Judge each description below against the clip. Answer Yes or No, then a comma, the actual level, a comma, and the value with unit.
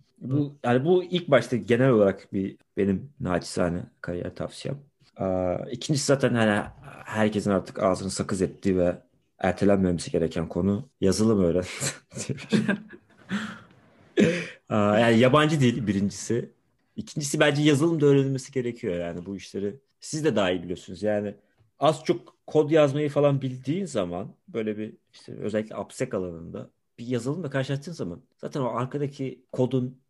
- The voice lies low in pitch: Yes, low, 120 Hz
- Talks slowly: No, average, 135 wpm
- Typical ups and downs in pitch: No, wide, 6.0 semitones